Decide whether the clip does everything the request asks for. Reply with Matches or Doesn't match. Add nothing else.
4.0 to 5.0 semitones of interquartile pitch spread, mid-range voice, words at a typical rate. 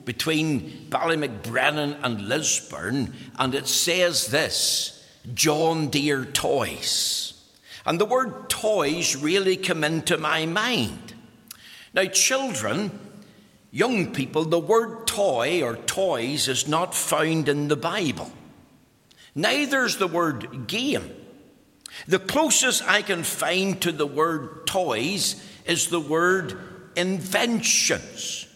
Doesn't match